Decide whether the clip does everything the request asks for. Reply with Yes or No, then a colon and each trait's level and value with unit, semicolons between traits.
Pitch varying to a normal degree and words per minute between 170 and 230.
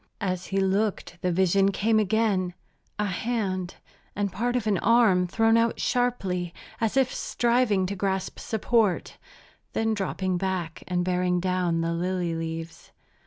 No: average, 3.5 semitones; average, 145 wpm